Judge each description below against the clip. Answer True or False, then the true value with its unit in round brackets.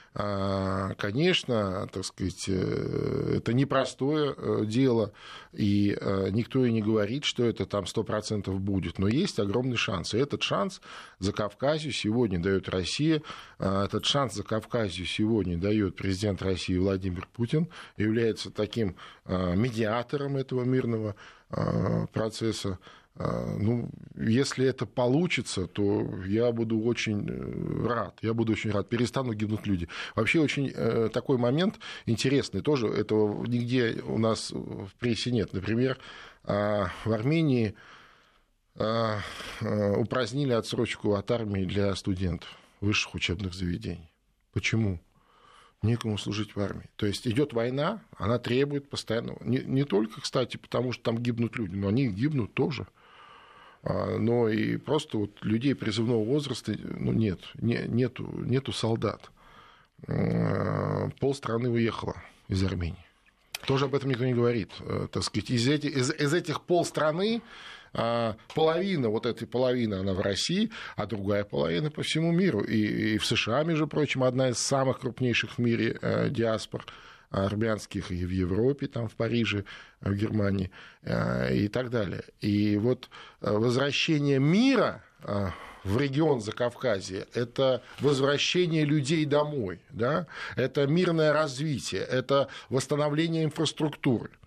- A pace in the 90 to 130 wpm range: True (125 wpm)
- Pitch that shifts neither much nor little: True (4.7 semitones)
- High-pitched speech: False (115 Hz)